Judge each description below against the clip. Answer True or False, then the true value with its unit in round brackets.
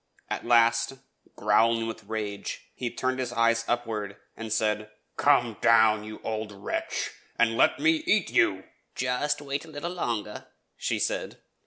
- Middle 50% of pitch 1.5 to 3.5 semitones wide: True (2.9 semitones)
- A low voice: True (115 Hz)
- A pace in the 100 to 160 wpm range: True (150 wpm)